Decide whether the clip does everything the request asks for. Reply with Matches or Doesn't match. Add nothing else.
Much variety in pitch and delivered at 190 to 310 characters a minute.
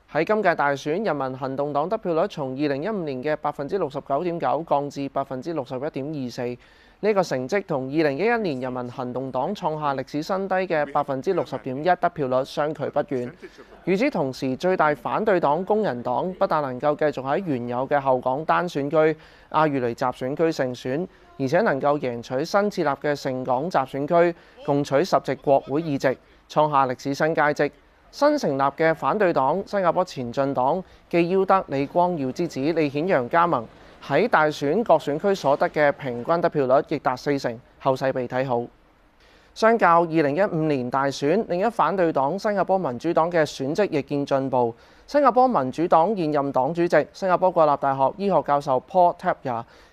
Doesn't match